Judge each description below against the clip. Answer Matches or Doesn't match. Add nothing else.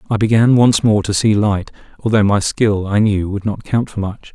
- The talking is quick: Matches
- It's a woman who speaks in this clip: Doesn't match